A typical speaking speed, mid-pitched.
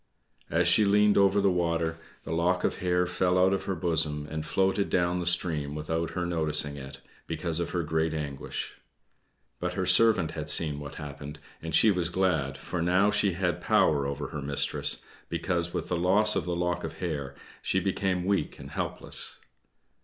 No: average, 185 wpm; very low, 85 Hz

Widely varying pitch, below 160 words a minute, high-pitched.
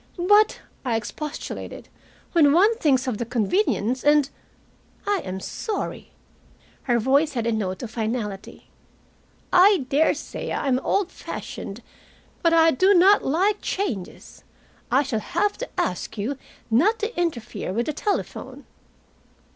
Yes: wide, 8.1 semitones; average, 140 wpm; very high, 280 Hz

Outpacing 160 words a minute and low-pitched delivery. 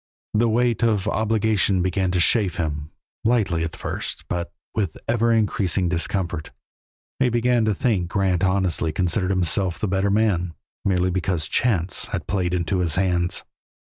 No: average, 155 wpm; very low, 95 Hz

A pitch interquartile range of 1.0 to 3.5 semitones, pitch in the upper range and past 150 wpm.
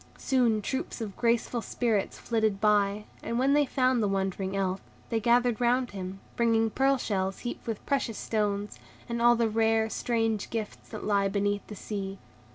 Yes: average, 2.9 semitones; high, 220 Hz; average, 170 wpm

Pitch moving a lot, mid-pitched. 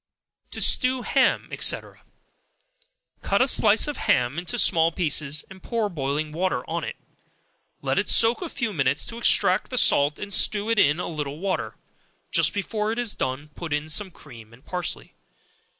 Yes: wide, 6.3 semitones; medium, 180 Hz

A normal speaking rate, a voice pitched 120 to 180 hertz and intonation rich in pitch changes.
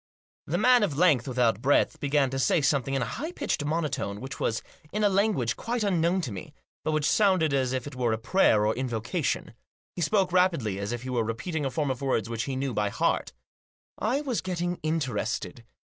No: fast, 210 wpm; medium, 140 Hz; wide, 6.7 semitones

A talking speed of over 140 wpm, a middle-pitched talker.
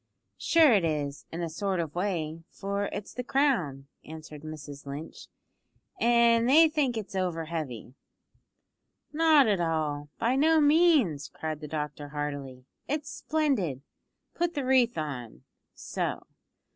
No: slow, 135 wpm; medium, 175 Hz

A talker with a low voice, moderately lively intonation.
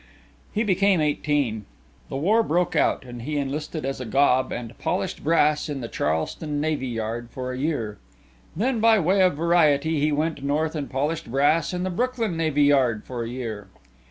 No: medium, 145 Hz; average, 4.4 semitones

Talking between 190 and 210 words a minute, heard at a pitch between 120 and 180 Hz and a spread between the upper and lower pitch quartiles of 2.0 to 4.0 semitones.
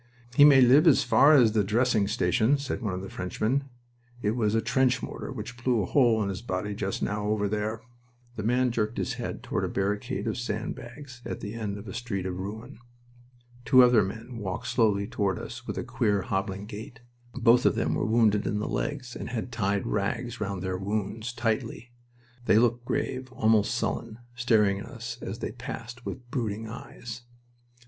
No: average, 195 wpm; low, 110 Hz; average, 3.1 semitones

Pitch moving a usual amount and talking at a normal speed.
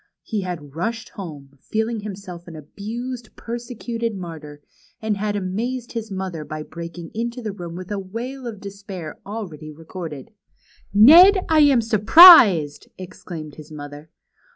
No: wide, 5.8 semitones; average, 145 wpm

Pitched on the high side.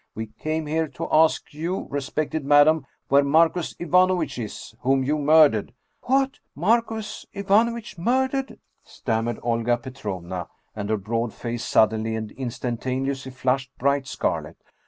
No: medium, 140 Hz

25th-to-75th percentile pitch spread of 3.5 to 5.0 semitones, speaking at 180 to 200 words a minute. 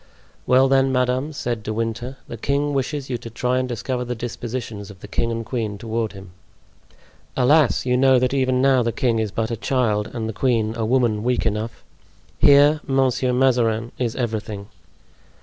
No: narrow, 2.6 semitones; average, 185 wpm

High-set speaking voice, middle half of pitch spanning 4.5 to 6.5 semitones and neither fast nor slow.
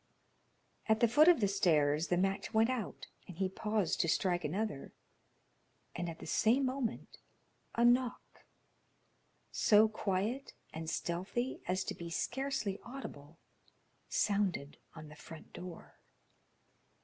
No: high, 195 Hz; wide, 5.6 semitones; slow, 130 wpm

